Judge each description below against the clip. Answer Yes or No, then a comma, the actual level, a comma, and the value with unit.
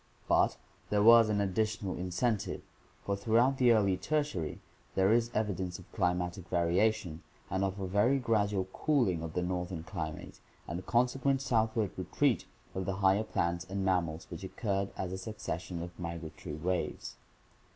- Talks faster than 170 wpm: No, average, 160 wpm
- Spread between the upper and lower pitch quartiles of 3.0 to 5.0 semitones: Yes, average, 3.8 semitones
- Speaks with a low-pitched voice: Yes, very low, 95 Hz